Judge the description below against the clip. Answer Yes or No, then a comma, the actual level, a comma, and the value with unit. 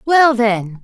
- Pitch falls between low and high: No, high, 240 Hz